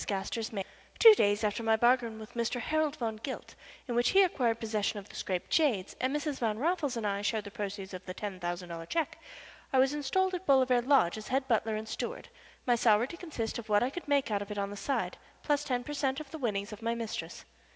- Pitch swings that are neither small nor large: Yes, average, 4.8 semitones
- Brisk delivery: Yes, fast, 245 wpm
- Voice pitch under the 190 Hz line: No, high, 230 Hz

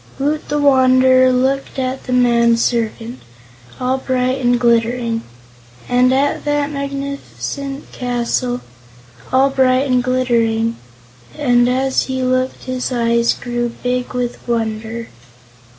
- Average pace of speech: No, slow, 120 wpm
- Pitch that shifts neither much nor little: No, narrow, 1.7 semitones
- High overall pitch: Yes, very high, 255 Hz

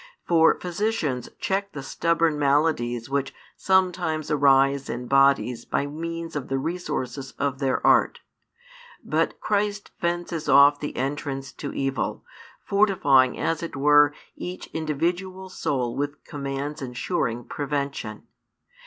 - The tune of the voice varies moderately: Yes, average, 3.6 semitones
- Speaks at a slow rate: Yes, slow, 120 wpm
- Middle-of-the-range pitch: Yes, medium, 145 Hz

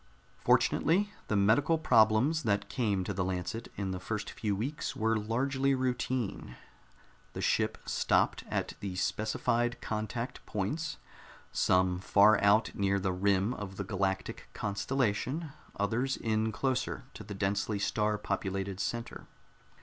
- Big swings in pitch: No, average, 3.7 semitones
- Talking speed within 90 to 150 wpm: Yes, slow, 135 wpm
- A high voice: No, low, 105 Hz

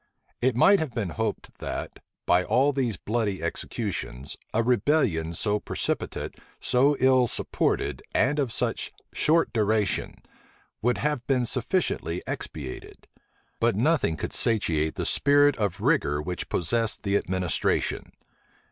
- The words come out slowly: Yes, slow, 130 wpm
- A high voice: No, low, 115 Hz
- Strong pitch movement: Yes, wide, 6.6 semitones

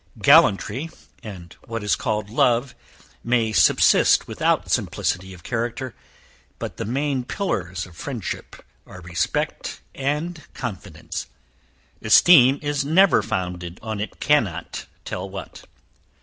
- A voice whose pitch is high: No, low, 115 Hz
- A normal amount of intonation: No, wide, 6.6 semitones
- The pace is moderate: No, slow, 115 wpm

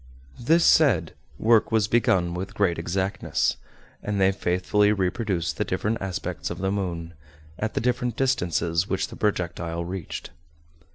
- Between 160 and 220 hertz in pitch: No, very low, 95 Hz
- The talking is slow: No, average, 145 wpm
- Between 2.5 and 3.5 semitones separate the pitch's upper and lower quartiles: No, average, 3.9 semitones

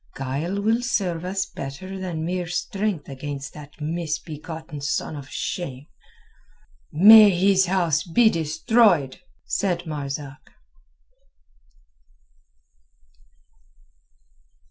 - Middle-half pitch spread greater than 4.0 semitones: Yes, average, 4.4 semitones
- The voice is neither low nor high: Yes, medium, 165 Hz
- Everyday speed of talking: No, slow, 85 wpm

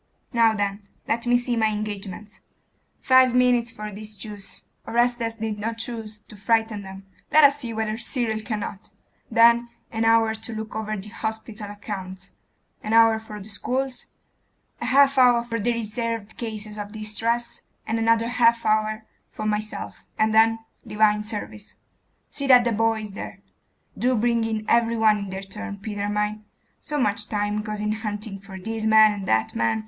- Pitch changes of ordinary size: No, narrow, 1.7 semitones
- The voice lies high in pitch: Yes, high, 220 Hz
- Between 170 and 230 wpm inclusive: Yes, average, 175 wpm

